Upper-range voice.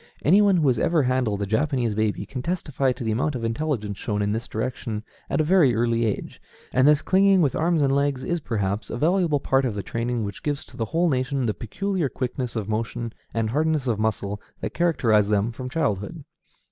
No: low, 125 Hz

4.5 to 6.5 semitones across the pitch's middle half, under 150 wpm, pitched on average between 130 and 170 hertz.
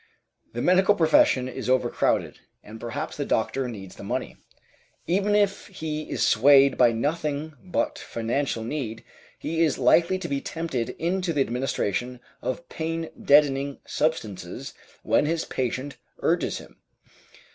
Yes: average, 4.8 semitones; slow, 135 wpm; medium, 140 Hz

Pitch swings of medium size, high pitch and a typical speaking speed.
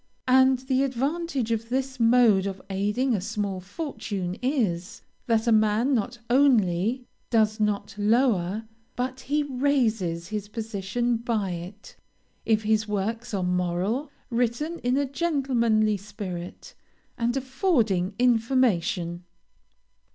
No: average, 4.2 semitones; high, 225 Hz; slow, 120 wpm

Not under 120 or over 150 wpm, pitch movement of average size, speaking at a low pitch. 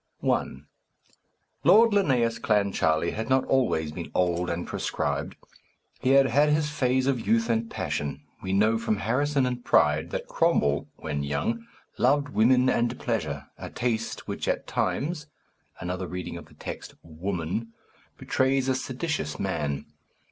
No: average, 145 wpm; wide, 6.9 semitones; low, 115 Hz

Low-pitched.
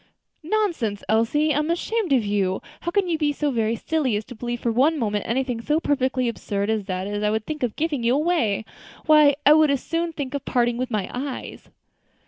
No: very high, 255 Hz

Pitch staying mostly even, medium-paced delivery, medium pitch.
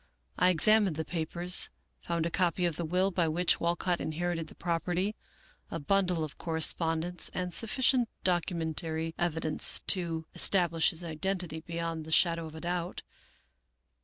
Yes: narrow, 1.9 semitones; average, 145 wpm; medium, 170 Hz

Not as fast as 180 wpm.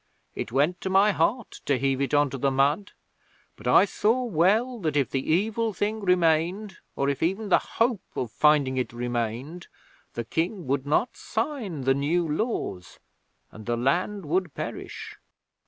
Yes: average, 170 wpm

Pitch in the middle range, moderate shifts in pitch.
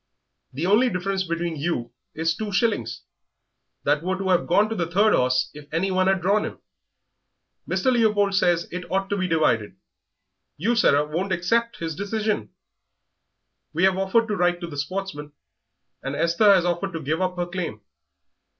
Yes: medium, 180 Hz; average, 3.4 semitones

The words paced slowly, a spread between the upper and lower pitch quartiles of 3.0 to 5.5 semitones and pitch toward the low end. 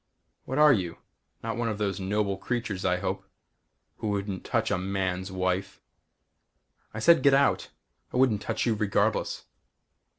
No: average, 155 wpm; average, 3.6 semitones; low, 100 Hz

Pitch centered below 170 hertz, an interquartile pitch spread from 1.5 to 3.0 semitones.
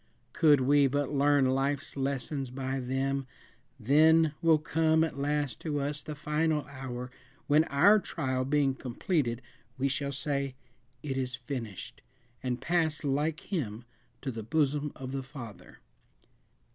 Yes: medium, 140 Hz; narrow, 2.4 semitones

